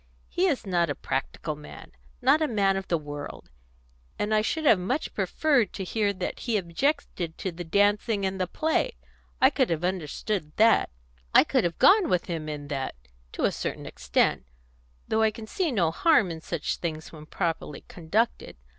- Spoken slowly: No, average, 185 wpm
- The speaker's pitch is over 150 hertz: Yes, high, 190 Hz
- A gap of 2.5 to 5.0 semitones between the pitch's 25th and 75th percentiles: No, wide, 5.6 semitones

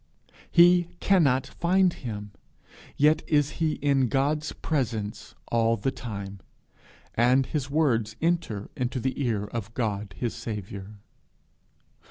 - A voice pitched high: No, low, 125 Hz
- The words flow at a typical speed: No, slow, 120 wpm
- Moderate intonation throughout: No, wide, 5.7 semitones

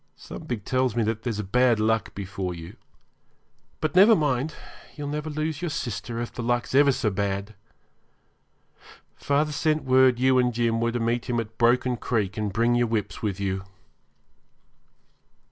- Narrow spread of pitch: No, average, 3.5 semitones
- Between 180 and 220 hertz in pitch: No, low, 120 Hz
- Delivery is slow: No, average, 160 wpm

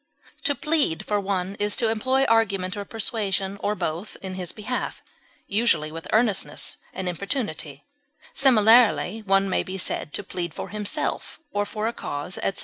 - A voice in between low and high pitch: No, high, 200 Hz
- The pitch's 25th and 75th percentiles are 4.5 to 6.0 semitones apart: No, average, 3.4 semitones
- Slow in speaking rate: No, average, 160 wpm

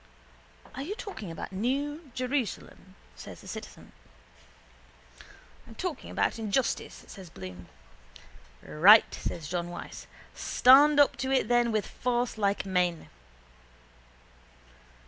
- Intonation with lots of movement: Yes, wide, 6.6 semitones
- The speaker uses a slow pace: Yes, slow, 115 wpm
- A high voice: Yes, high, 230 Hz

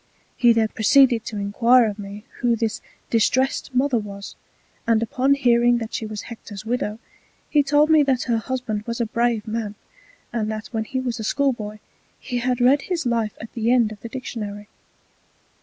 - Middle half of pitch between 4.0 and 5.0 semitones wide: No, average, 2.7 semitones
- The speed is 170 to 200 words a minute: Yes, average, 185 wpm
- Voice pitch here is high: Yes, high, 235 Hz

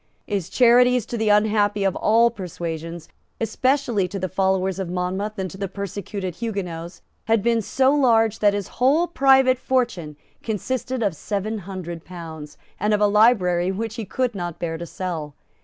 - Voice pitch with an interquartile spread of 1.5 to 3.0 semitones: No, average, 4.3 semitones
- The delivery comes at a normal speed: Yes, average, 170 wpm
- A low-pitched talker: No, high, 205 Hz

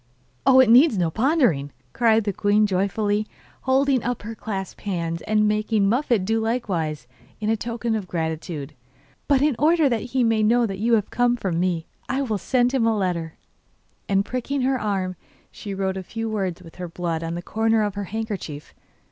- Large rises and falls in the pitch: No, average, 4.4 semitones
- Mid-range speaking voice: No, high, 215 Hz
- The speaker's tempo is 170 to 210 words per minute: Yes, average, 190 wpm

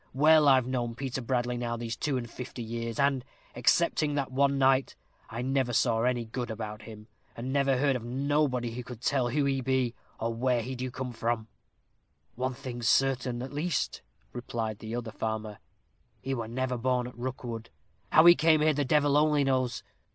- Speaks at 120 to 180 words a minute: No, average, 190 wpm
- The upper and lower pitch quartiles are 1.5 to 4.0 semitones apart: Yes, narrow, 2.4 semitones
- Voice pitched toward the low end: Yes, low, 125 Hz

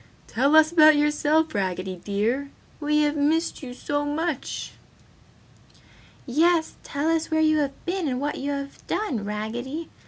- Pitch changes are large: No, average, 3.7 semitones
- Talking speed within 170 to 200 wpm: No, average, 150 wpm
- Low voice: No, very high, 290 Hz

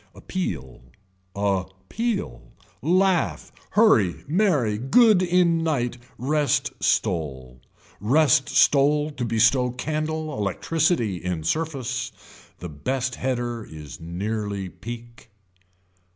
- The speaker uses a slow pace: Yes, slow, 95 wpm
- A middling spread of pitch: No, wide, 7.6 semitones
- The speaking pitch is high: No, low, 125 Hz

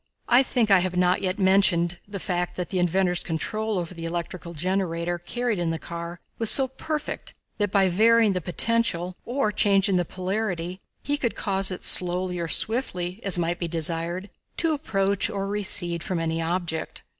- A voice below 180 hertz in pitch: No, medium, 185 Hz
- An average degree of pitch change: Yes, average, 3.1 semitones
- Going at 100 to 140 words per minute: No, average, 180 wpm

